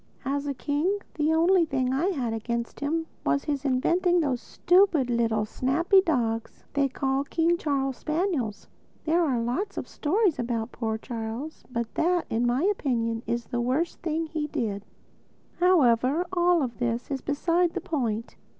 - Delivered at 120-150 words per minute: No, average, 160 wpm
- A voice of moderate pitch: No, very high, 275 Hz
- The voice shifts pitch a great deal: Yes, wide, 5.9 semitones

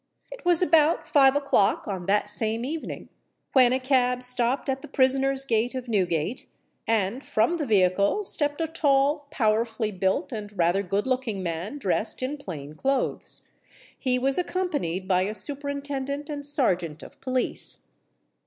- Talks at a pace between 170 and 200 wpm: No, average, 155 wpm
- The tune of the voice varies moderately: No, wide, 5.8 semitones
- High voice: Yes, very high, 255 Hz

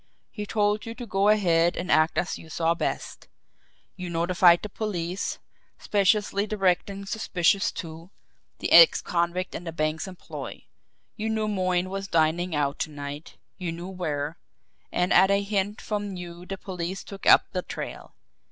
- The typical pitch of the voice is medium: Yes, medium, 180 Hz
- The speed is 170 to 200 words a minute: No, average, 160 wpm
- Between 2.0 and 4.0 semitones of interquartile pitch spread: Yes, average, 2.9 semitones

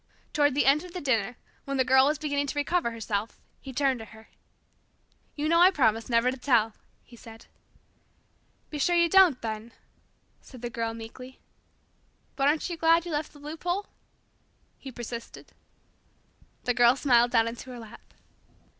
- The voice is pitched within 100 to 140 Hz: No, very high, 260 Hz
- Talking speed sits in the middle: Yes, average, 170 wpm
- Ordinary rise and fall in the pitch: Yes, average, 4.5 semitones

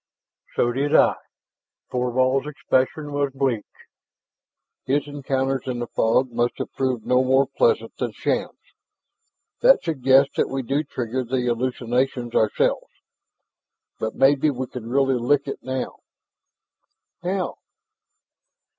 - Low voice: Yes, low, 130 Hz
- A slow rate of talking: Yes, slow, 120 wpm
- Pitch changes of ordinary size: No, narrow, 2.1 semitones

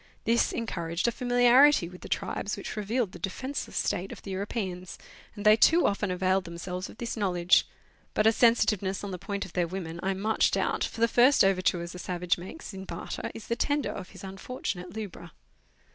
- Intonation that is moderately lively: Yes, average, 4.0 semitones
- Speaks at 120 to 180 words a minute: No, average, 200 wpm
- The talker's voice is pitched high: Yes, high, 195 Hz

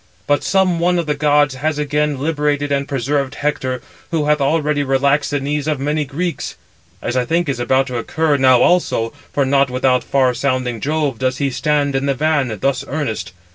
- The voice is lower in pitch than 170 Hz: Yes, medium, 140 Hz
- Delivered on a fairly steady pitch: Yes, narrow, 2.3 semitones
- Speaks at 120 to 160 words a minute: No, average, 195 wpm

